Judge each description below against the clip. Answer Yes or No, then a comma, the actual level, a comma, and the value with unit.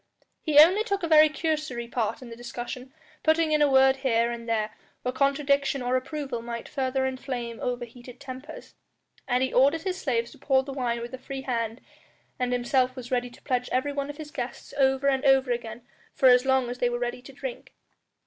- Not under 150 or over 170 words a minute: No, fast, 205 wpm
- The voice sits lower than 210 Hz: No, very high, 260 Hz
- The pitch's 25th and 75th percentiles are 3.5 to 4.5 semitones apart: No, narrow, 2.5 semitones